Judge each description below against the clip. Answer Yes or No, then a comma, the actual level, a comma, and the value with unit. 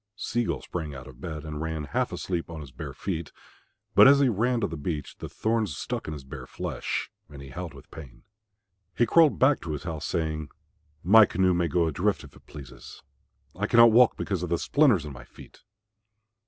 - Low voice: Yes, very low, 85 Hz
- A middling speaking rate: No, fast, 210 wpm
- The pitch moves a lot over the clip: Yes, wide, 6.5 semitones